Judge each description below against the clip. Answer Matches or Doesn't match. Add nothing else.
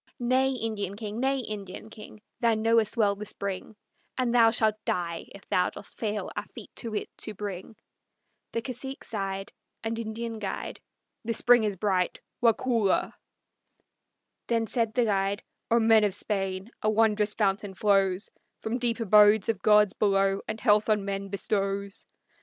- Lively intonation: Doesn't match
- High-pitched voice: Matches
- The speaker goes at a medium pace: Matches